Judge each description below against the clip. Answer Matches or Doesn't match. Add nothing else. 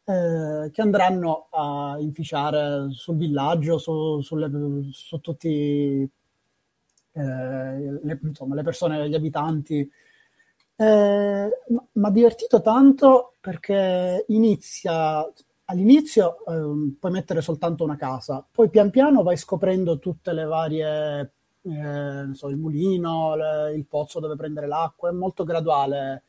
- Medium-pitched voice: Matches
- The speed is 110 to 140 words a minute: Matches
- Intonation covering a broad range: Doesn't match